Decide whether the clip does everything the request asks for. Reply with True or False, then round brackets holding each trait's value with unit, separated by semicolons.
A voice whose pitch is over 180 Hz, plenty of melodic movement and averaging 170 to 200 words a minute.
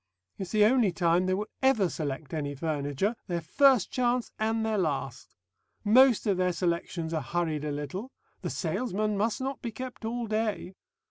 True (190 Hz; 5.7 semitones; 175 wpm)